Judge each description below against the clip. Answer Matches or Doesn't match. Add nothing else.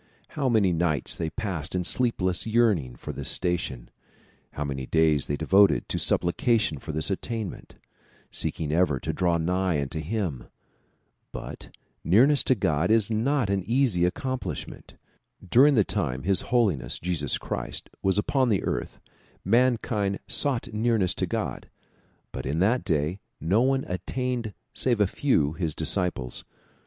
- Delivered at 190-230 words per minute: Doesn't match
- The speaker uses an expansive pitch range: Matches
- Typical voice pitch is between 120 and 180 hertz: Doesn't match